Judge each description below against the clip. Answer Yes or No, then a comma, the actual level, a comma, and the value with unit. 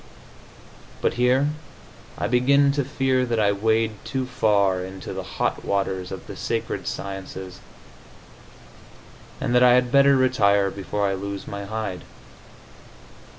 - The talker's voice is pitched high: No, low, 110 Hz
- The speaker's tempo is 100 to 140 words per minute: Yes, slow, 135 wpm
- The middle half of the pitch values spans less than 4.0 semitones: No, average, 4.3 semitones